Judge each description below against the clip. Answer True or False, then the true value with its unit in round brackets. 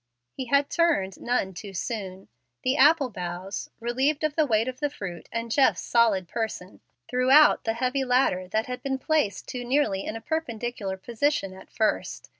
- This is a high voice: True (240 Hz)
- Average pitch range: False (5.7 semitones)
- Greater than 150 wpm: True (180 wpm)